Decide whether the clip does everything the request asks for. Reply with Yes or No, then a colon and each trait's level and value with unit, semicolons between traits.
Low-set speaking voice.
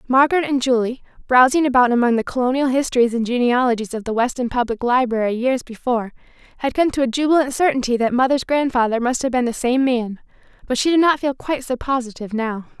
No: very high, 250 Hz